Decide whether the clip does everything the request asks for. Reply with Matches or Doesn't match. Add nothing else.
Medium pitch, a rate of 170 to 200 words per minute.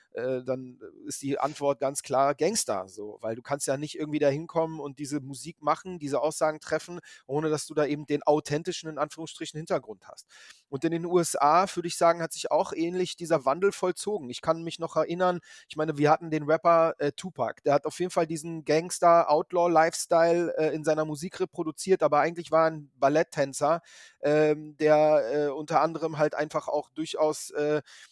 Matches